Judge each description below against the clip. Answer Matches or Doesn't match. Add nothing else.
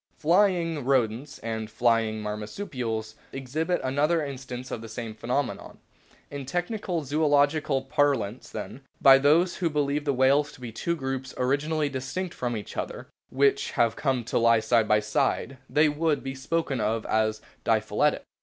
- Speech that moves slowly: Doesn't match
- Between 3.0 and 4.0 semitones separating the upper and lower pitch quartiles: Doesn't match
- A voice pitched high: Doesn't match